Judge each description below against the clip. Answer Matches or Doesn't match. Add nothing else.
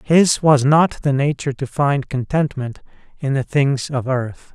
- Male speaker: Matches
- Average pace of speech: Matches